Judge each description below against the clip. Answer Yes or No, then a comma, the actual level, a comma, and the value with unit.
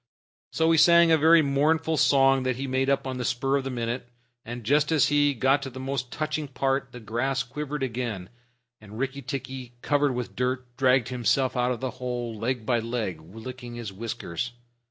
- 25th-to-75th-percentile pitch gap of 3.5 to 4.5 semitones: No, narrow, 2.5 semitones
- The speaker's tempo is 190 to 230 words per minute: Yes, average, 195 wpm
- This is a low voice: Yes, low, 130 Hz